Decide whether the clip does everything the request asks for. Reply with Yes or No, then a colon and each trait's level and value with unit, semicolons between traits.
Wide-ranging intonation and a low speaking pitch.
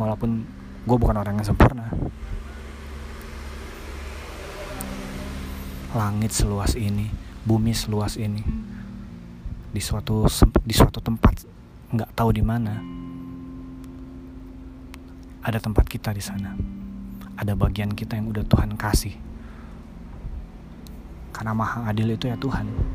Yes: wide, 7.1 semitones; low, 100 Hz